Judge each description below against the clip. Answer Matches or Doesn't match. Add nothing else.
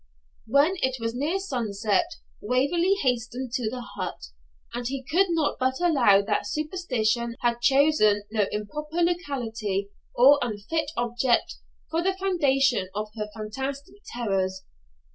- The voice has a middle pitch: Doesn't match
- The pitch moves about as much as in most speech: Doesn't match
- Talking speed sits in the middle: Doesn't match